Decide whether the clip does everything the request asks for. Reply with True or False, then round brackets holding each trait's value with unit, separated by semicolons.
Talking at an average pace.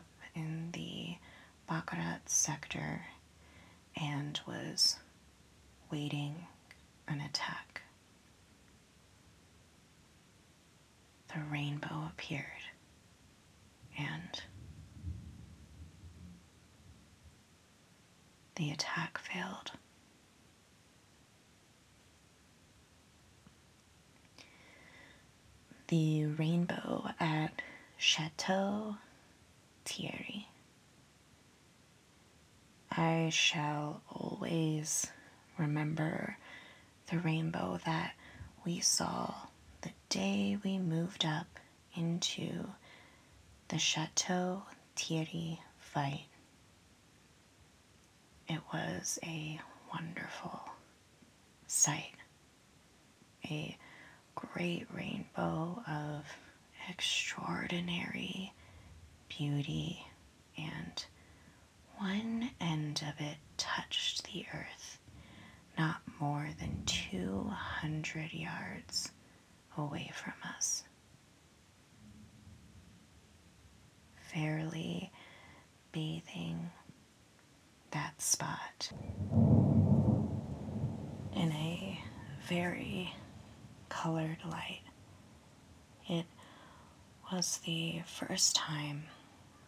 False (55 wpm)